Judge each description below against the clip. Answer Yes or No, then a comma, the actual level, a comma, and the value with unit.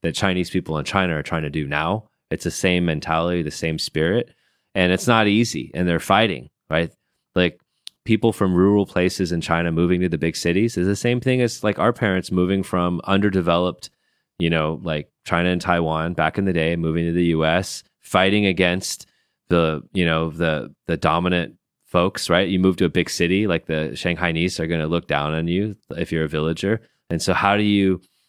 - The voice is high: No, very low, 90 Hz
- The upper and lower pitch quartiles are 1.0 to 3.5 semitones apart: Yes, average, 2.7 semitones